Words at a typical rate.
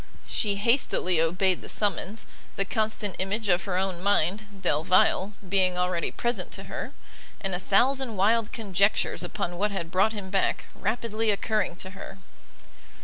Yes: average, 150 wpm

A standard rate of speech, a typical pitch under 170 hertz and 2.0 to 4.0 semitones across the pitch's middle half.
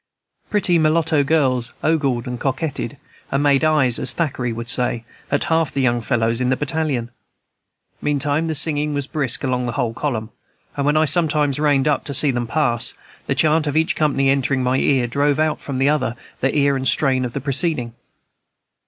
Yes: average, 190 wpm; medium, 140 Hz; average, 3.2 semitones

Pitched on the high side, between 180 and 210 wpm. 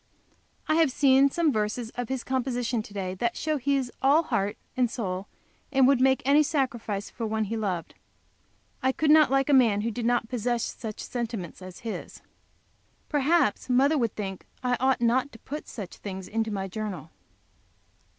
Yes: high, 240 Hz; average, 185 wpm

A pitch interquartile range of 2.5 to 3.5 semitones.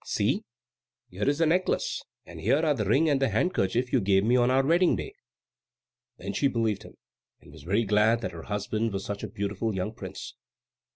No: average, 5.2 semitones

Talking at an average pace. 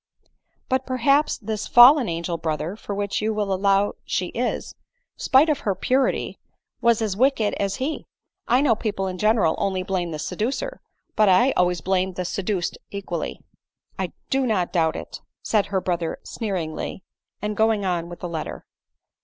Yes: average, 175 wpm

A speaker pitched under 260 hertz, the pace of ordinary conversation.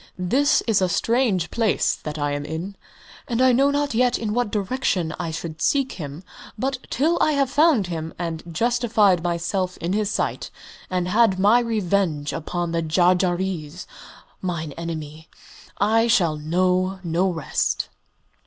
Yes: medium, 185 Hz; average, 150 wpm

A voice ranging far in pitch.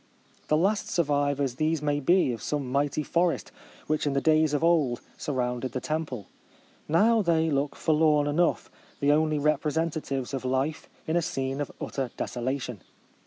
No: average, 2.8 semitones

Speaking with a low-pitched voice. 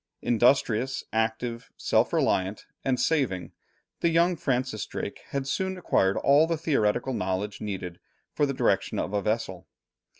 Yes: low, 120 Hz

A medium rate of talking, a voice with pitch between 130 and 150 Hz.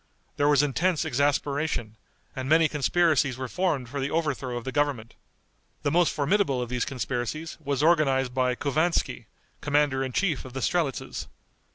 Yes: average, 160 wpm; medium, 140 Hz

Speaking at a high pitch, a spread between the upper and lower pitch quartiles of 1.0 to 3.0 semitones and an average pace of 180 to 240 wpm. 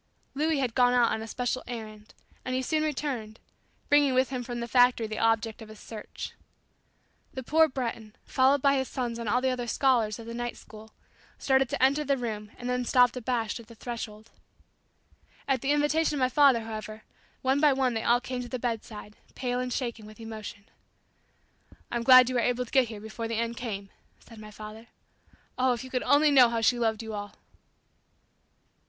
Yes: high, 245 Hz; average, 2.7 semitones; fast, 205 wpm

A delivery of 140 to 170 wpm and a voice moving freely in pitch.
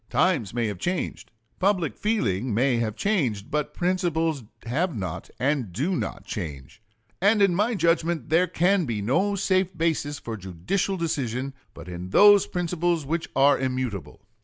Yes: average, 155 wpm; wide, 7.8 semitones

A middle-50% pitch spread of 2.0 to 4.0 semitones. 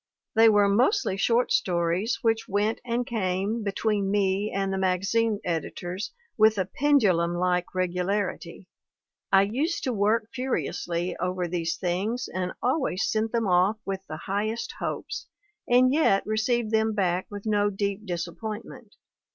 Yes: average, 3.5 semitones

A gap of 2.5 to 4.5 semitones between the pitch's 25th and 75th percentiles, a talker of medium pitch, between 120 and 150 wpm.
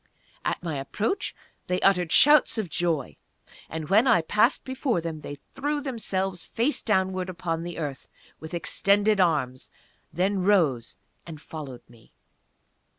No: average, 4.9 semitones; medium, 180 Hz; average, 140 wpm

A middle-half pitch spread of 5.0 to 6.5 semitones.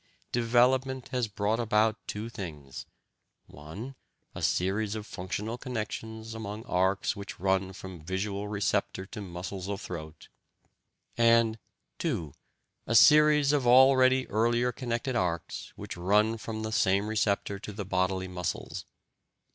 No: average, 3.8 semitones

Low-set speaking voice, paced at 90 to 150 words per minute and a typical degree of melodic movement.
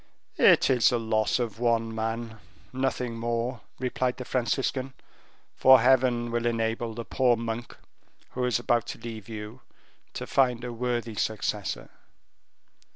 No: low, 120 Hz; average, 140 wpm; narrow, 1.7 semitones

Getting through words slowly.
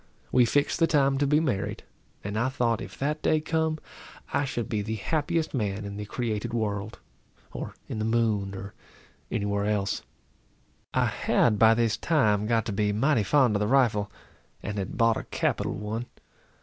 No: average, 185 wpm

